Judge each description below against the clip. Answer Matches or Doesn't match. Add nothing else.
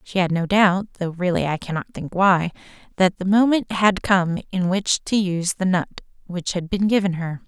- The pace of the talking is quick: Matches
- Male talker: Doesn't match